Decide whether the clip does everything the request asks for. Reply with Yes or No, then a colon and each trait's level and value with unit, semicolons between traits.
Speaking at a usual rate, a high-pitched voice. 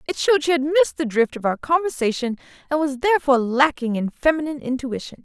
Yes: average, 195 wpm; very high, 280 Hz